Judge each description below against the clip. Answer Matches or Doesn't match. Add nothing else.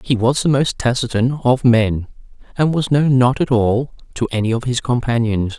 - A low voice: Matches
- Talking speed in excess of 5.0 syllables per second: Doesn't match